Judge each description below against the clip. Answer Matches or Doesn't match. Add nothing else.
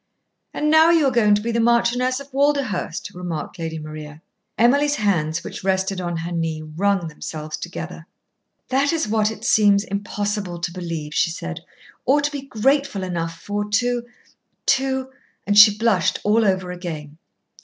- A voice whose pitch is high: Matches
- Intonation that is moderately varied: Doesn't match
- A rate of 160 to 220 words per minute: Matches